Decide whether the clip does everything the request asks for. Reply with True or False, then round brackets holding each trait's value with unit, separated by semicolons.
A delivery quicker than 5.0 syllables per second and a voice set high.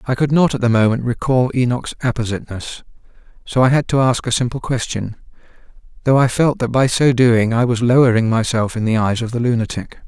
False (5.8 syllables/s; 120 Hz)